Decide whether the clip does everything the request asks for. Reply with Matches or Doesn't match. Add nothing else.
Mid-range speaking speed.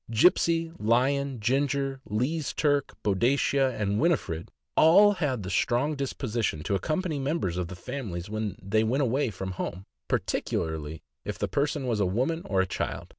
Matches